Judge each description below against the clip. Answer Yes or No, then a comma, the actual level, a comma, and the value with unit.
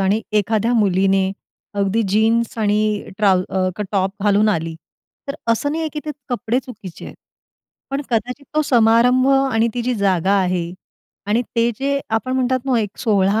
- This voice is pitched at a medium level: No, high, 220 Hz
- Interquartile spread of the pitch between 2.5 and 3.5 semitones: No, average, 4.1 semitones